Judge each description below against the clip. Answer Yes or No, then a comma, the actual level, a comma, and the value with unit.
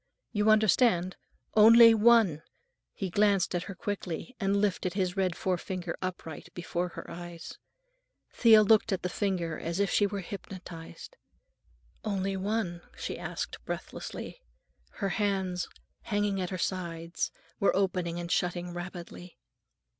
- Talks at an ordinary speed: No, slow, 130 wpm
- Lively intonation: No, average, 2.8 semitones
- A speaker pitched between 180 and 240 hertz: Yes, medium, 185 Hz